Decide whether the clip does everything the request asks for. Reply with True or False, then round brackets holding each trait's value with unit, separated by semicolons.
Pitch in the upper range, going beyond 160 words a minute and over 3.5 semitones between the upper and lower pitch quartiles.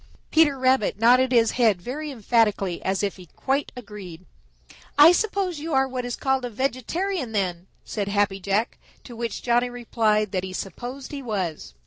True (235 Hz; 175 wpm; 4.8 semitones)